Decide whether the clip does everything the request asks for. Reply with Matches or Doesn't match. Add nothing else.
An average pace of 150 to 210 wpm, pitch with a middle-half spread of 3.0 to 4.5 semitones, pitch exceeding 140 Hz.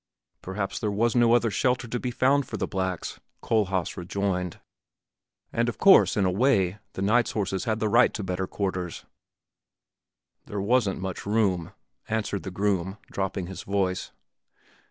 Doesn't match